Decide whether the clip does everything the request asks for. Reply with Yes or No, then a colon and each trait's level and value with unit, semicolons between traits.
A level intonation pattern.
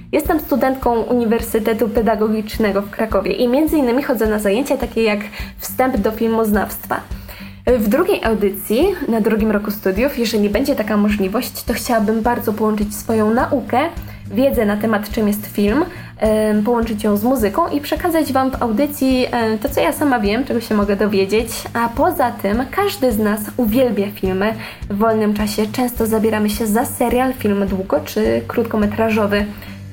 No: average, 3.2 semitones